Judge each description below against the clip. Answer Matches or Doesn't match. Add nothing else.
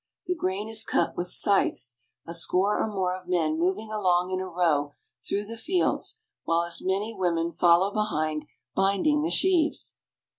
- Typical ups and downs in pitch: Matches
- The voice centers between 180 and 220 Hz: Matches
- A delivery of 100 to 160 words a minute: Doesn't match